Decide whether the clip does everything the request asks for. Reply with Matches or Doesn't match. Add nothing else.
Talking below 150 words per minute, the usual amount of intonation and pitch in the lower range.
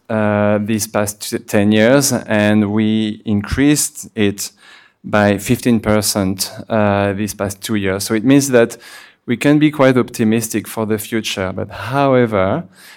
Doesn't match